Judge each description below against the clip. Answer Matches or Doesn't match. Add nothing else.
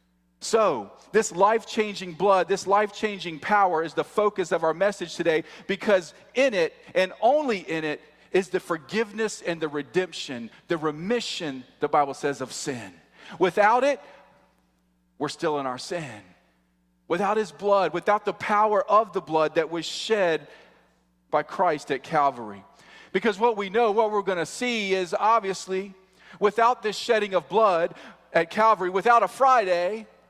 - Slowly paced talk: Doesn't match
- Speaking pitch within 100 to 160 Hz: Doesn't match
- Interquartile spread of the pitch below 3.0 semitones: Doesn't match